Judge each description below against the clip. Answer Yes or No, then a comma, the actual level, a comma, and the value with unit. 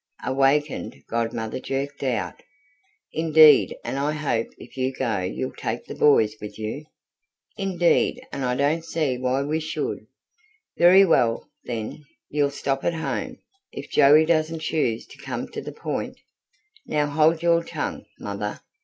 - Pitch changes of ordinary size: Yes, average, 4.2 semitones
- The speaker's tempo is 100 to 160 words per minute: Yes, average, 150 wpm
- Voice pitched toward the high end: No, medium, 140 Hz